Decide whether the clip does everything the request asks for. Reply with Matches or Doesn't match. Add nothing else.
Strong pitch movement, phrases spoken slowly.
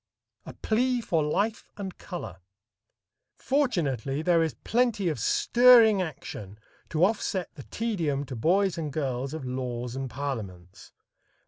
Matches